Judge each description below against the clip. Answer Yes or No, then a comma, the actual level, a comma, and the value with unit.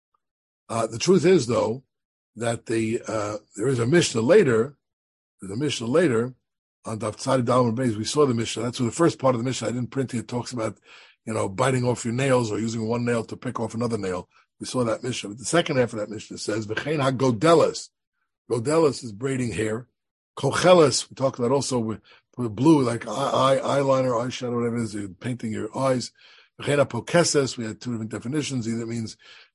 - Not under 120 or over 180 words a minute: No, fast, 205 wpm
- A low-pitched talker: Yes, low, 120 Hz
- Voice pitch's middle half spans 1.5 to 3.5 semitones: Yes, average, 3.1 semitones